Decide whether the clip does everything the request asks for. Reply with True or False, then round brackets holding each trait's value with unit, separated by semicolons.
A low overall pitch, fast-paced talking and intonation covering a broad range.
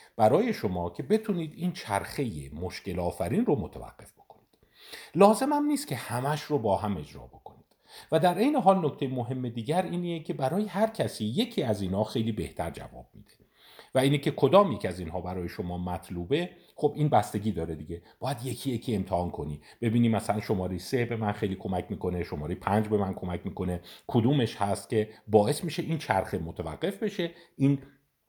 True (115 Hz; 180 wpm; 8.2 semitones)